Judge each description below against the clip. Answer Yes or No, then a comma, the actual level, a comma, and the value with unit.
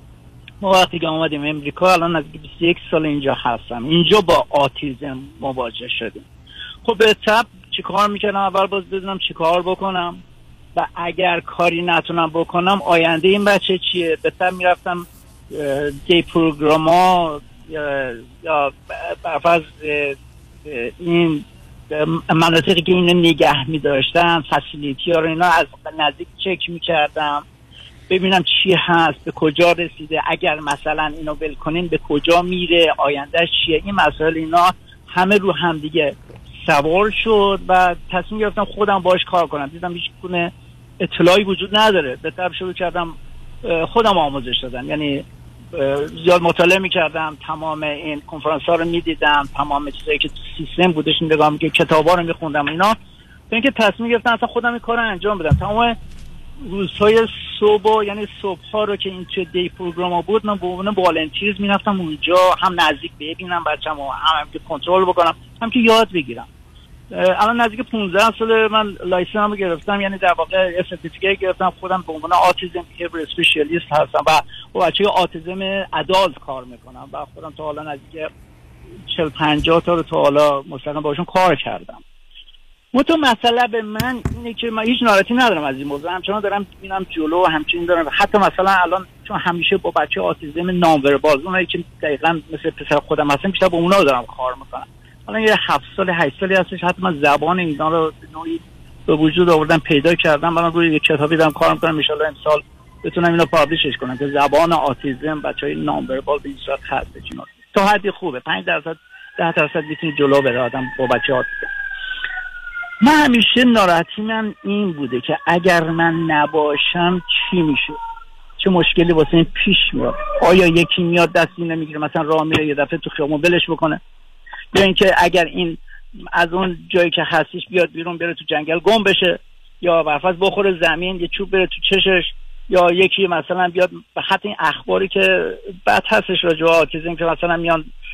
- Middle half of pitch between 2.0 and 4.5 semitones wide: Yes, average, 3.7 semitones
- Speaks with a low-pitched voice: No, medium, 170 Hz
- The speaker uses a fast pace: Yes, fast, 165 wpm